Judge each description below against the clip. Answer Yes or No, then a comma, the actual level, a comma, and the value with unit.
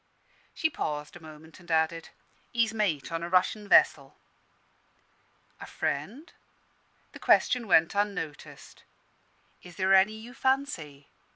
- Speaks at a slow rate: Yes, slow, 120 wpm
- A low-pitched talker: No, medium, 180 Hz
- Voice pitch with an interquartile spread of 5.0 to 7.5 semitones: Yes, average, 5.3 semitones